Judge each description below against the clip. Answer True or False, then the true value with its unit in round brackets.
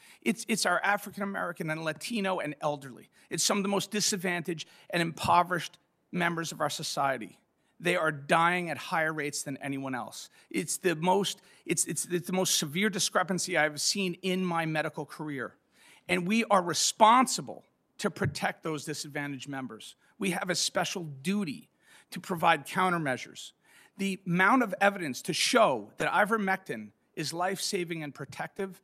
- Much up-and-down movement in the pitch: False (3.8 semitones)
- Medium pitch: True (175 Hz)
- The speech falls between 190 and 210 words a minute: False (160 wpm)